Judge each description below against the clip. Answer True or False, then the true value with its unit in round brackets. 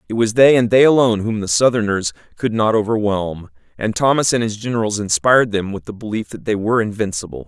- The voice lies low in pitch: True (105 Hz)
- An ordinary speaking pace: False (210 wpm)